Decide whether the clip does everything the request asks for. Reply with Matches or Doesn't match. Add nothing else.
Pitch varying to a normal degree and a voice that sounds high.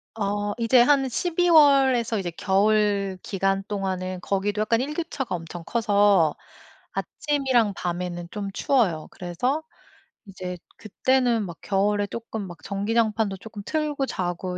Matches